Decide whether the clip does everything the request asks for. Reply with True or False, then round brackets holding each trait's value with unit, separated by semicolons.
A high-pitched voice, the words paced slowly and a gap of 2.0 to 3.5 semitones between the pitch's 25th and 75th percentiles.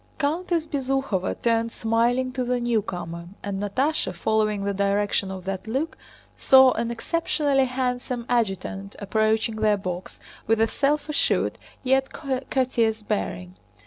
False (230 Hz; 130 wpm; 4.6 semitones)